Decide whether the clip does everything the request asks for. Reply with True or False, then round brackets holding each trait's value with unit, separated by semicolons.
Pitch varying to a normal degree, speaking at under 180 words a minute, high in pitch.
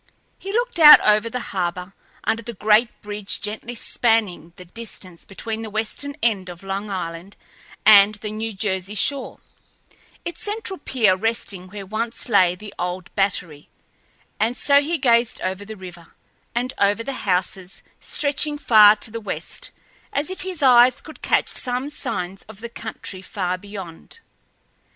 True (4.2 semitones; 155 wpm; 215 Hz)